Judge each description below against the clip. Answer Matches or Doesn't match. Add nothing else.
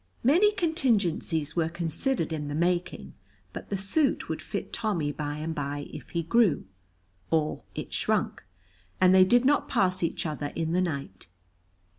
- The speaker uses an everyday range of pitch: Doesn't match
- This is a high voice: Doesn't match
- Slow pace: Doesn't match